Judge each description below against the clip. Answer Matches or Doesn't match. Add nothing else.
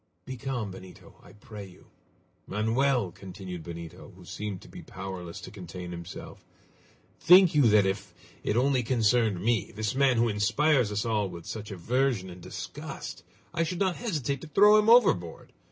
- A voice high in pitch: Doesn't match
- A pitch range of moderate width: Doesn't match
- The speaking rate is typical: Matches